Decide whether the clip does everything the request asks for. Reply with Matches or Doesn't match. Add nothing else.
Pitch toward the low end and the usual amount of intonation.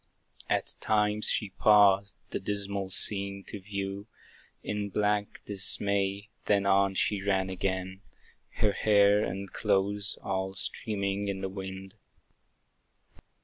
Doesn't match